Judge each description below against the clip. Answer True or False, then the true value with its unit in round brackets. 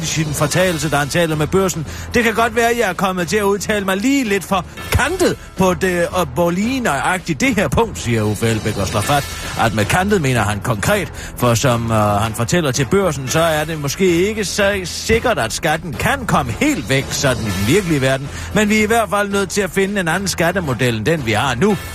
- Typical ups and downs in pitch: False (7.4 semitones)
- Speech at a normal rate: False (240 wpm)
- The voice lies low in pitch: False (170 Hz)